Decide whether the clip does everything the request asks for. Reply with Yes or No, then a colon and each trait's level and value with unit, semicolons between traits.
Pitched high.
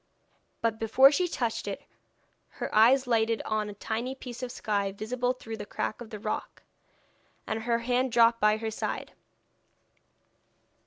Yes: high, 230 Hz